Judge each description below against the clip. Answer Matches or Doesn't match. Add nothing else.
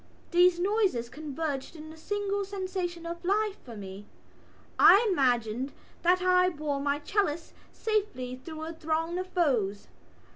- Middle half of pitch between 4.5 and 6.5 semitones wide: Matches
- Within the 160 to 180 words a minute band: Doesn't match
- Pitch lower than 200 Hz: Doesn't match